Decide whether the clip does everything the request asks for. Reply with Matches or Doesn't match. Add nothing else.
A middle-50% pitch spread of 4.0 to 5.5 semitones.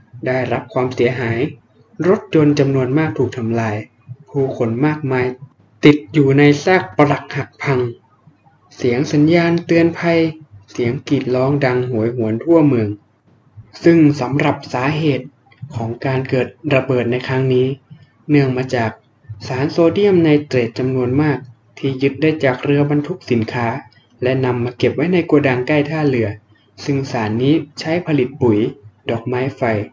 Doesn't match